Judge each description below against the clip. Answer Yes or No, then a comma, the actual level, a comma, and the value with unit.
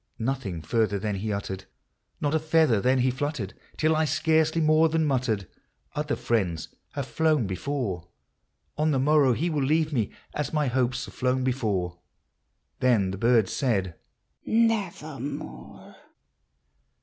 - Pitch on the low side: Yes, low, 130 Hz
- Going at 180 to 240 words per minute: No, average, 150 wpm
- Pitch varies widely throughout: Yes, wide, 6.3 semitones